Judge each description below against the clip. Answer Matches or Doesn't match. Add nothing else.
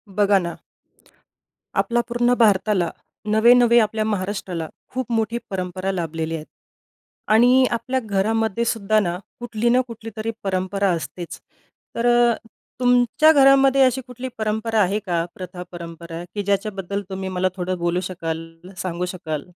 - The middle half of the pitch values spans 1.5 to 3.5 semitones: Doesn't match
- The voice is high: Matches